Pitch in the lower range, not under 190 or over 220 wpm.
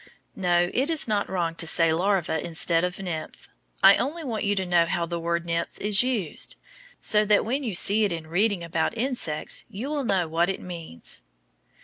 No: medium, 185 Hz; average, 200 wpm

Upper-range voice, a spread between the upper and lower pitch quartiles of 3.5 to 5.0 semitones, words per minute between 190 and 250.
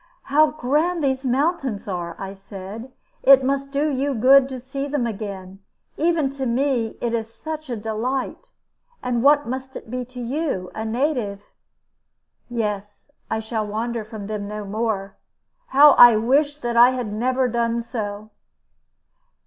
No: high, 240 Hz; average, 4.1 semitones; average, 155 wpm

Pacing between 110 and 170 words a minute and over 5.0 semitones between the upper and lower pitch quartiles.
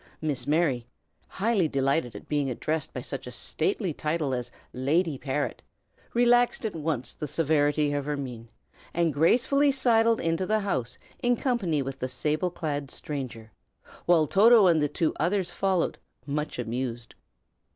Yes: average, 150 wpm; wide, 5.6 semitones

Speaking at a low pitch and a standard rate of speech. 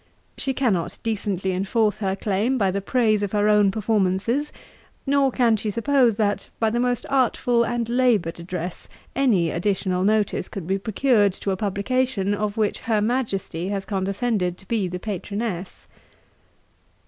No: high, 210 Hz; average, 155 wpm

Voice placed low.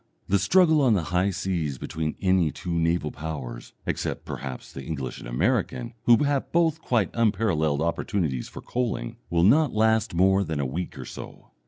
Yes: very low, 90 Hz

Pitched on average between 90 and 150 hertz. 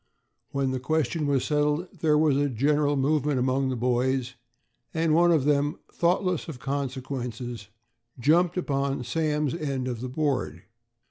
Yes: medium, 140 Hz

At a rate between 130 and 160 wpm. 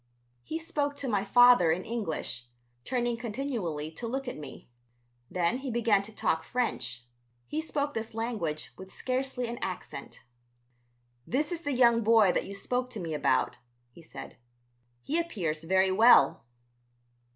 Yes: average, 150 wpm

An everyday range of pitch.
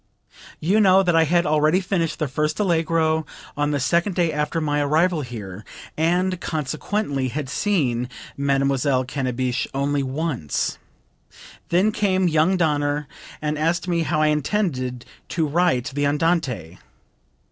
Yes: average, 3.8 semitones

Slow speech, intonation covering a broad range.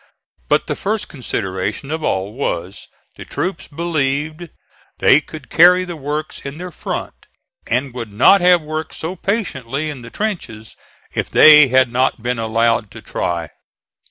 No: average, 155 wpm; wide, 5.9 semitones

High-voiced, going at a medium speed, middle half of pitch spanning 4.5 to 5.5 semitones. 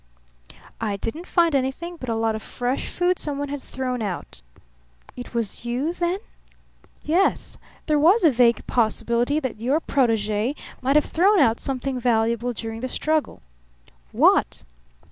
Yes: very high, 255 Hz; average, 145 wpm; average, 4.9 semitones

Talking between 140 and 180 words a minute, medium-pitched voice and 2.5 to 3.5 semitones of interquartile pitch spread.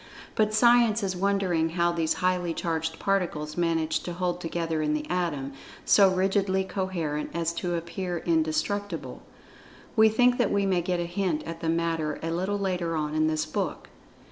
Yes: average, 170 wpm; medium, 175 Hz; average, 2.9 semitones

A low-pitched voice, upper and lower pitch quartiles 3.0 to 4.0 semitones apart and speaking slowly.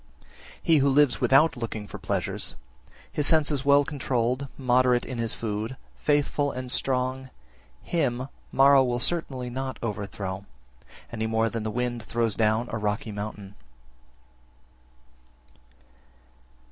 Yes: low, 125 Hz; average, 3.5 semitones; slow, 125 wpm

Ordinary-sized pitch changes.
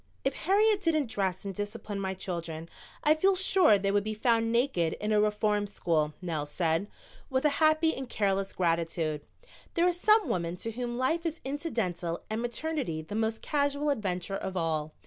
No: wide, 8.2 semitones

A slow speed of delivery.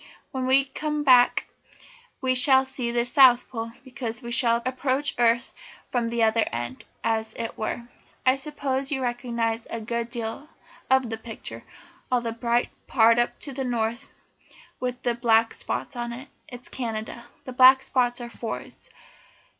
No: average, 165 wpm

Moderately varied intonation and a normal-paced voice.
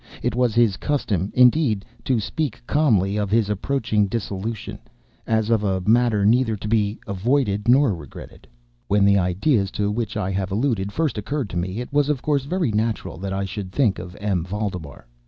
Yes: average, 3.9 semitones; average, 185 wpm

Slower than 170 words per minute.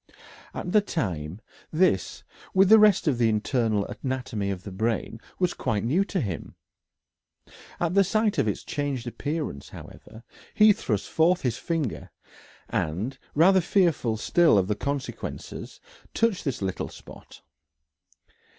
Yes: average, 140 wpm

